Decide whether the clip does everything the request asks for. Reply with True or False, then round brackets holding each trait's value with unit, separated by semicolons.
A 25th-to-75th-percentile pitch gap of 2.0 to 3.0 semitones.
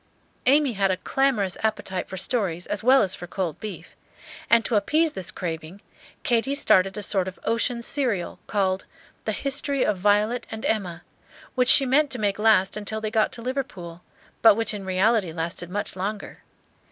False (4.1 semitones)